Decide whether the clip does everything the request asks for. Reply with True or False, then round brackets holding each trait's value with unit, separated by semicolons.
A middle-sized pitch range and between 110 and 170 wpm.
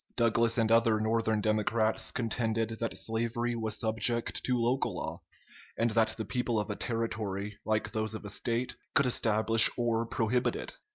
False (1.3 semitones; 165 wpm)